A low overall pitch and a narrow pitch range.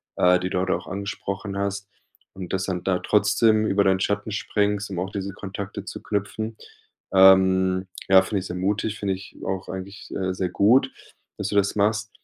Yes: low, 100 Hz; narrow, 1.5 semitones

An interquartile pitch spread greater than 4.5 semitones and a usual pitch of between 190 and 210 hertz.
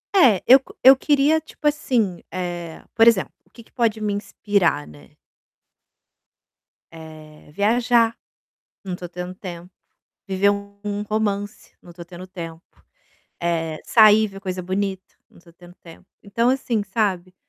No: average, 4.0 semitones; high, 195 Hz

